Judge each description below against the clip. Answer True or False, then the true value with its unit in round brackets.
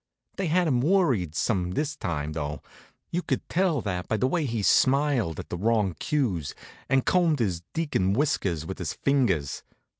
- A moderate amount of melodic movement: False (9.0 semitones)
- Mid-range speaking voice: False (120 Hz)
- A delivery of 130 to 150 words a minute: False (175 wpm)